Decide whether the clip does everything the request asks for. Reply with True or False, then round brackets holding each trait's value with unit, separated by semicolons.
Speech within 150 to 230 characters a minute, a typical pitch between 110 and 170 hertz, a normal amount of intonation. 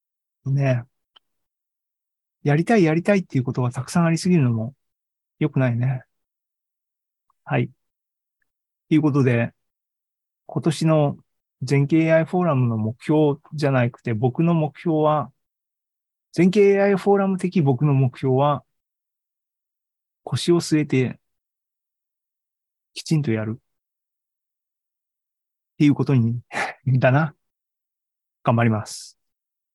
True (210 characters per minute; 140 Hz; 4.1 semitones)